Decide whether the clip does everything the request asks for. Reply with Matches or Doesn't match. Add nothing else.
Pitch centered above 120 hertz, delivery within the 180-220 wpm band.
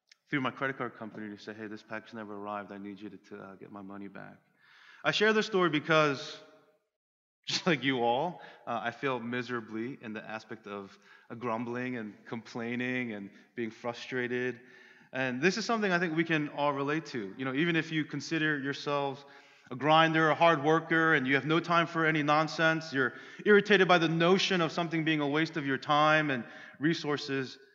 Matches